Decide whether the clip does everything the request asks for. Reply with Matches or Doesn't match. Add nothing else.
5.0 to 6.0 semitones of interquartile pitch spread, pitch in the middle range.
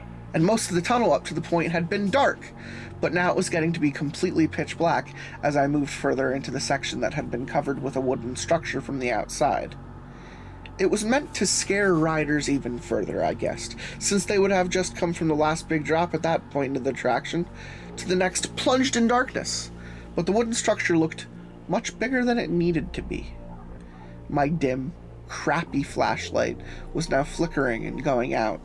Matches